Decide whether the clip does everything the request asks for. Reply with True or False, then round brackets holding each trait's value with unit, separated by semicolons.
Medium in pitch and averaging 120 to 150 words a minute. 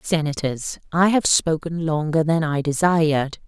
True (160 Hz; 140 wpm)